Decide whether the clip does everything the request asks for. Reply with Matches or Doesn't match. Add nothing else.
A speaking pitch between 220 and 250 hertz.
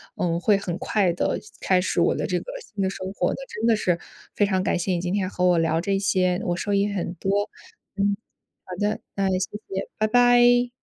Doesn't match